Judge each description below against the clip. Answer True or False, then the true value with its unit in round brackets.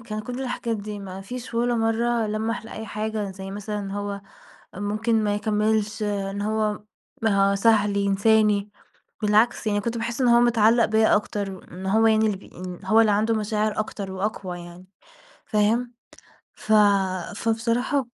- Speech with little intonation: True (1.9 semitones)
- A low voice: False (215 Hz)